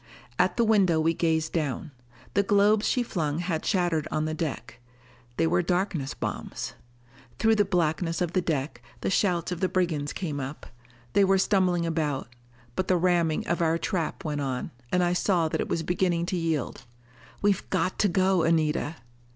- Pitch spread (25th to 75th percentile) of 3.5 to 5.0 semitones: No, average, 2.9 semitones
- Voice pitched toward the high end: No, medium, 170 Hz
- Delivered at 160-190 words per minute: Yes, average, 180 wpm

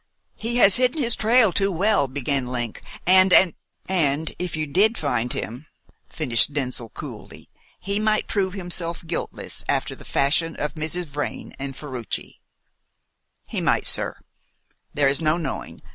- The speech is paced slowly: No, average, 155 wpm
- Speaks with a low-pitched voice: No, medium, 160 Hz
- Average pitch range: No, wide, 5.8 semitones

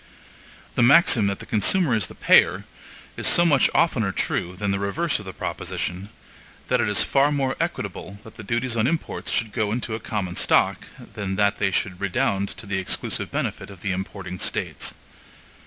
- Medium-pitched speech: No, low, 105 Hz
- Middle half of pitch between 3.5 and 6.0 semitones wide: Yes, average, 3.9 semitones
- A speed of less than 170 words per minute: No, average, 190 wpm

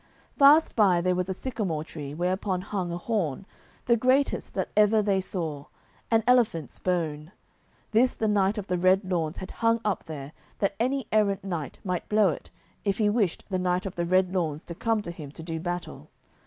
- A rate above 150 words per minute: Yes, average, 200 wpm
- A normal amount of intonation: Yes, average, 3.7 semitones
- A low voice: No, medium, 185 Hz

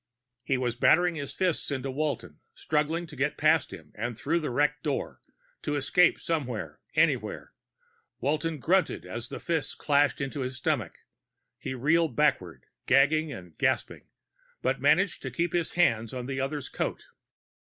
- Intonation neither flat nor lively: Yes, average, 3.8 semitones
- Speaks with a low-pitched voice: No, medium, 145 Hz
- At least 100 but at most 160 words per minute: Yes, average, 155 wpm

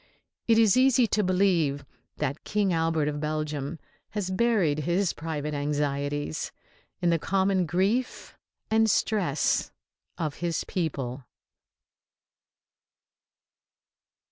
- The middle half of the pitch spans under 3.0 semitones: No, average, 5.1 semitones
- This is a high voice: No, medium, 165 Hz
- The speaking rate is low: Yes, slow, 100 wpm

